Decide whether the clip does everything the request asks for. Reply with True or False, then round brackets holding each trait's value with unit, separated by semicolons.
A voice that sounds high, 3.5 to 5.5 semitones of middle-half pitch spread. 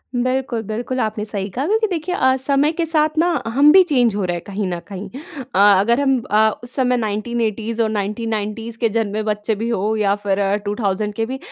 True (225 Hz; 3.8 semitones)